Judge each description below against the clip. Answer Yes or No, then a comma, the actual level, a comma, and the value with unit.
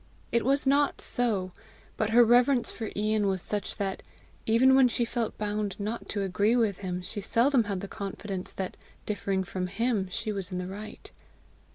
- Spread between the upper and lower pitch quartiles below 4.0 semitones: Yes, average, 3.3 semitones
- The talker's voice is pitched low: No, high, 210 Hz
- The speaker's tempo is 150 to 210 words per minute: Yes, average, 185 wpm